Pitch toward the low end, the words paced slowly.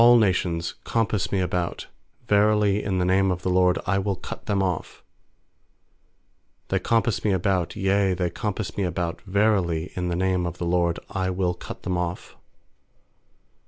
No: very low, 95 Hz; average, 165 wpm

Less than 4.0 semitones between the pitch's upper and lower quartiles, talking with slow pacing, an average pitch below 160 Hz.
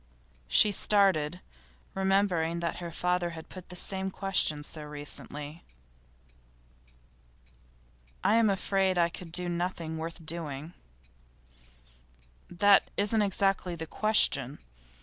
No: average, 3.2 semitones; slow, 105 wpm; medium, 175 Hz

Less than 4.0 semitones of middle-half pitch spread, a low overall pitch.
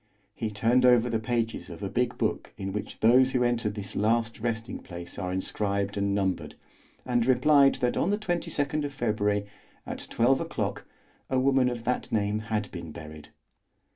Yes: average, 3.6 semitones; low, 115 Hz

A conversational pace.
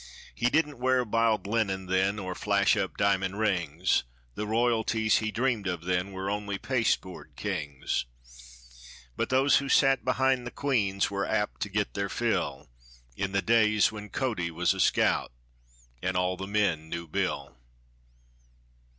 Yes: average, 150 wpm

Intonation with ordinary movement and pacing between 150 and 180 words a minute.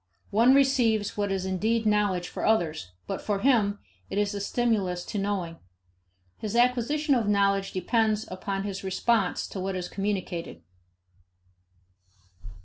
No: average, 3.0 semitones; average, 140 wpm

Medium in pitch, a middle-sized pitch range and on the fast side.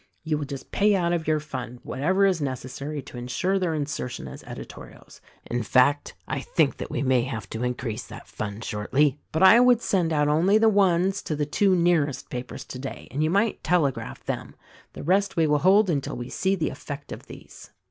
No: medium, 150 Hz; wide, 6.1 semitones; fast, 210 wpm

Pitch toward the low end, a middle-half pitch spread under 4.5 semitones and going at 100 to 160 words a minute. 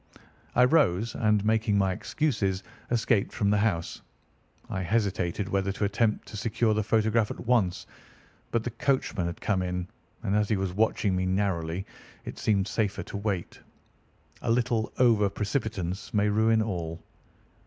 Yes: low, 105 Hz; average, 2.8 semitones; average, 155 wpm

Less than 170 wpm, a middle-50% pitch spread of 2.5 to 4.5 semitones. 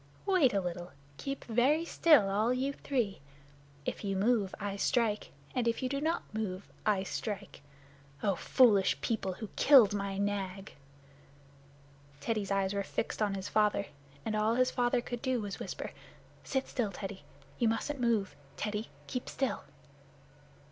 Yes: average, 155 wpm; average, 4.0 semitones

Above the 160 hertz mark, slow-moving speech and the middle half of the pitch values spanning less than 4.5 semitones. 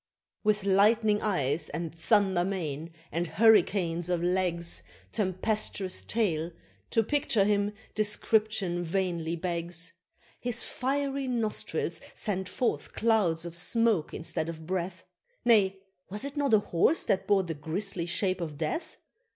Yes: high, 190 Hz; slow, 130 wpm; average, 4.1 semitones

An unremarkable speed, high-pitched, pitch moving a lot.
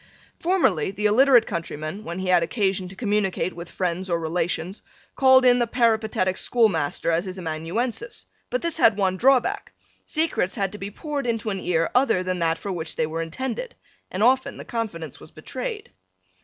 Yes: average, 185 wpm; high, 195 Hz; wide, 6.1 semitones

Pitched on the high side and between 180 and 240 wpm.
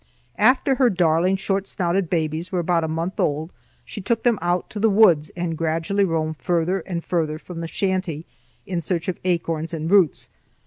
No: medium, 175 Hz; average, 185 wpm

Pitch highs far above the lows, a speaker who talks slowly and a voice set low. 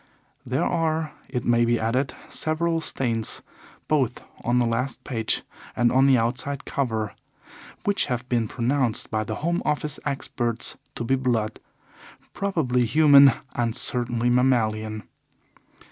No: average, 3.4 semitones; slow, 130 wpm; low, 125 Hz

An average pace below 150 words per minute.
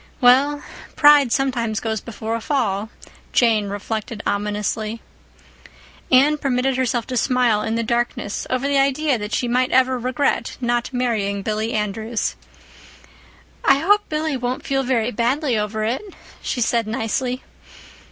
Yes: average, 140 wpm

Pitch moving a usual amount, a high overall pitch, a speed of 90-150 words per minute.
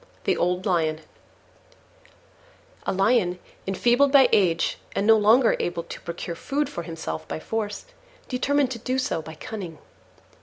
No: wide, 6.4 semitones; high, 195 Hz; average, 145 wpm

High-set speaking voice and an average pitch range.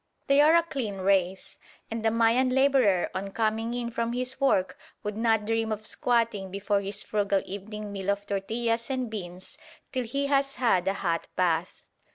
Yes: high, 220 Hz; average, 3.6 semitones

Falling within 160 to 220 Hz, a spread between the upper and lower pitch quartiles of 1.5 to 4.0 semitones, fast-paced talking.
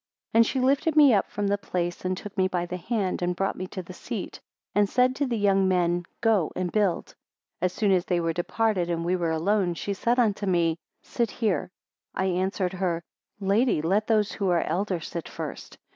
Yes: high, 190 Hz; average, 3.3 semitones; fast, 220 wpm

